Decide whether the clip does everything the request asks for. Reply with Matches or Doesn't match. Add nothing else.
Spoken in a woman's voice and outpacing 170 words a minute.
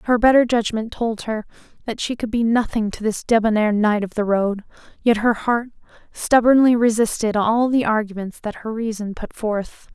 Matches